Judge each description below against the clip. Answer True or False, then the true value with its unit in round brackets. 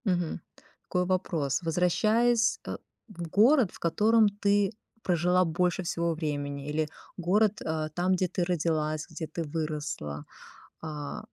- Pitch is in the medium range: True (175 Hz)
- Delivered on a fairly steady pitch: False (3.3 semitones)